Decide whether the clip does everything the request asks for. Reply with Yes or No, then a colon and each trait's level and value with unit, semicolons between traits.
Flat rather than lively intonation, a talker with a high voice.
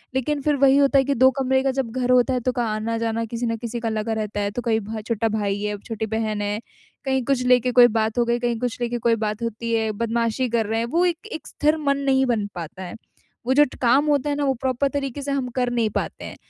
No: average, 3.2 semitones; high, 235 Hz